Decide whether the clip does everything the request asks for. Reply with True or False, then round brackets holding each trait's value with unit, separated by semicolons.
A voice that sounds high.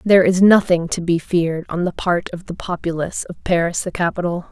False (175 Hz)